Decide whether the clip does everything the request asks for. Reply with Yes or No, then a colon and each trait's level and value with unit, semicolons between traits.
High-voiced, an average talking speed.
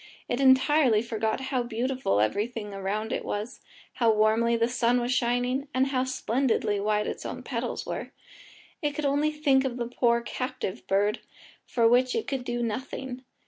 Yes: high, 245 Hz; average, 170 wpm